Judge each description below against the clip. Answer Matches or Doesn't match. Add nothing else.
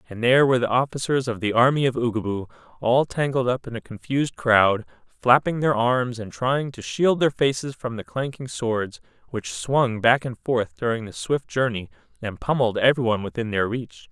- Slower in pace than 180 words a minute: Doesn't match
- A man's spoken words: Matches